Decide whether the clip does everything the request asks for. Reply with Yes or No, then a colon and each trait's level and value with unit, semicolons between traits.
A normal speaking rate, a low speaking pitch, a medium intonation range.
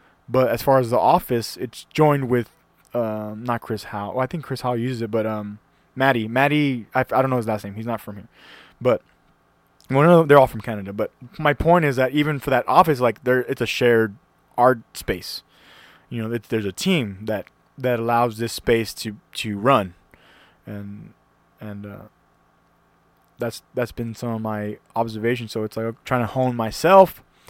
Yes: average, 195 wpm; low, 115 Hz; average, 3.3 semitones